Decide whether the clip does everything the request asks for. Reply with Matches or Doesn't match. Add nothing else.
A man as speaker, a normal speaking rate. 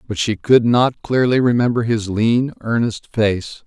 Matches